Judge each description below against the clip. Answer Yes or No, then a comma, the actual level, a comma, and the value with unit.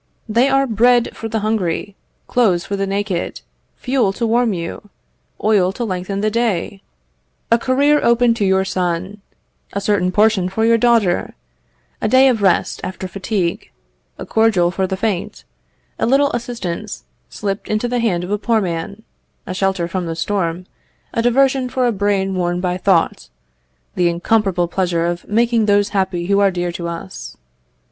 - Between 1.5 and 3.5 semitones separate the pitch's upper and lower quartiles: No, average, 4.0 semitones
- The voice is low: No, high, 200 Hz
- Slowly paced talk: No, average, 170 wpm